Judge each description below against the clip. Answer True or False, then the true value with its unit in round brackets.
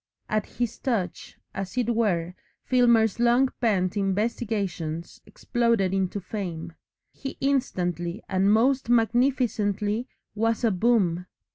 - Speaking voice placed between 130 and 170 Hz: False (215 Hz)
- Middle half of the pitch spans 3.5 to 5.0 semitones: True (4.3 semitones)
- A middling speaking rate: False (110 wpm)